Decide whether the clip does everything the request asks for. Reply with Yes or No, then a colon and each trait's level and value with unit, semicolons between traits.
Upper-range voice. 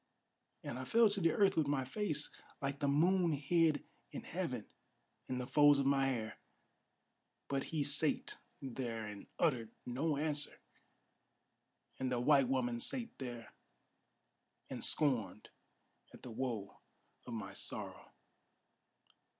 No: medium, 140 Hz